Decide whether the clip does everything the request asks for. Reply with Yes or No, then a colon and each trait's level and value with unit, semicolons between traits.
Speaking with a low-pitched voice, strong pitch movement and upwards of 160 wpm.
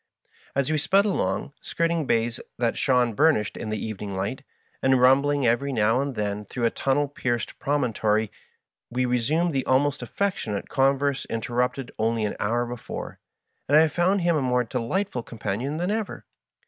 No: low, 130 Hz; average, 4.1 semitones; average, 170 wpm